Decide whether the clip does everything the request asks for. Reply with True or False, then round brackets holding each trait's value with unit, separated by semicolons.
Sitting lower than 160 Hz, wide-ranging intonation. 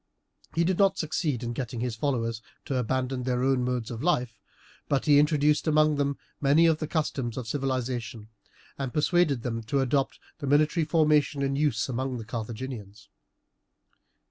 False (135 Hz; 3.7 semitones)